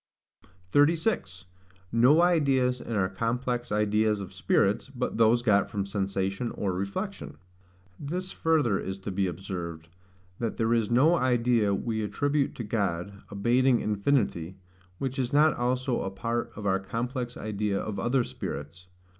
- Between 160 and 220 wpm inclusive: No, average, 145 wpm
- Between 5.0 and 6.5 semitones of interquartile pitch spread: No, average, 4.6 semitones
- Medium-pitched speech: No, low, 115 Hz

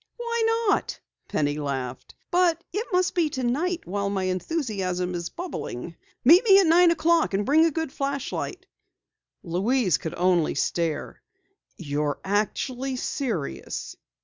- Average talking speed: No, slow, 130 wpm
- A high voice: Yes, very high, 255 Hz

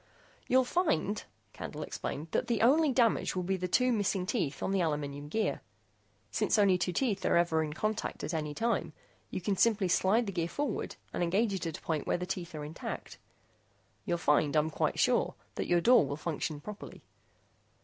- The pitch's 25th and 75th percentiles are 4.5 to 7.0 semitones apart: Yes, wide, 5.5 semitones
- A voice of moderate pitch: Yes, medium, 180 Hz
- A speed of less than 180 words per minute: No, average, 195 wpm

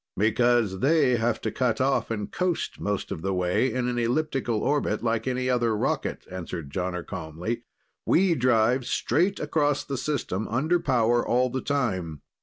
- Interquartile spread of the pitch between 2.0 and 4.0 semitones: No, average, 4.5 semitones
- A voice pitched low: Yes, low, 120 Hz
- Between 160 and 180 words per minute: Yes, average, 165 wpm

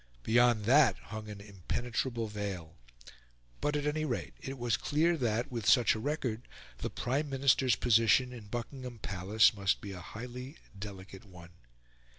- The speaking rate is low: No, average, 155 wpm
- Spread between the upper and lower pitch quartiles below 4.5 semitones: Yes, average, 4.0 semitones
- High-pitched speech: No, low, 115 Hz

